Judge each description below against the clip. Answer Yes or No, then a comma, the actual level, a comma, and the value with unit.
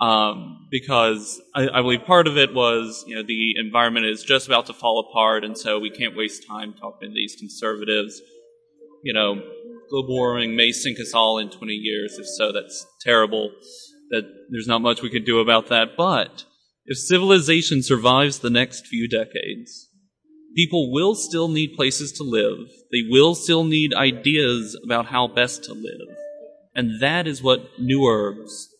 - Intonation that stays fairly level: No, wide, 5.5 semitones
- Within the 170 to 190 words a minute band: Yes, average, 175 wpm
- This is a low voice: Yes, low, 125 Hz